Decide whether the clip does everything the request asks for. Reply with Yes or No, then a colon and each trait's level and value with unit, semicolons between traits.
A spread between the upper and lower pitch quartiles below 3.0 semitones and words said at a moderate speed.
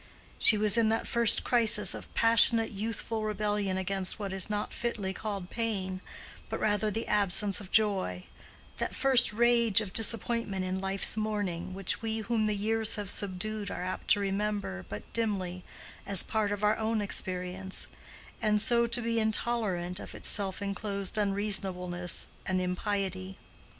Yes: narrow, 2.6 semitones; average, 155 wpm